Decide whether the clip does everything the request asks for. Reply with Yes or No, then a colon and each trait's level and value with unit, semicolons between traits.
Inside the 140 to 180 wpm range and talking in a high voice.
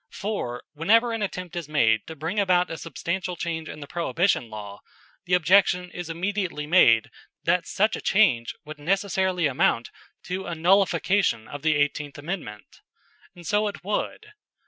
No: average, 160 wpm; medium, 175 Hz